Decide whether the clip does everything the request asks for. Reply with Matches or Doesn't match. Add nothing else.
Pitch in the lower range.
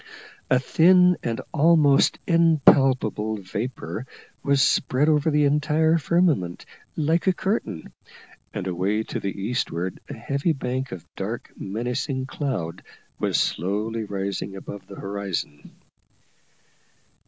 Matches